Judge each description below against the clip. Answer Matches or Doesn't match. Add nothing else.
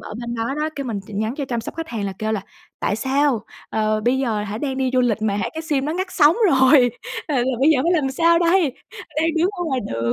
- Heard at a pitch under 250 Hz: Doesn't match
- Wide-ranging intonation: Matches